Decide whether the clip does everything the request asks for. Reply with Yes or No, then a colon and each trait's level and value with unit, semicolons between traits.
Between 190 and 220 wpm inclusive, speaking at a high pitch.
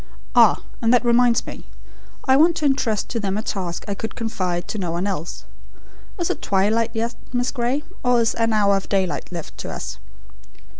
Yes: average, 195 wpm; high, 225 Hz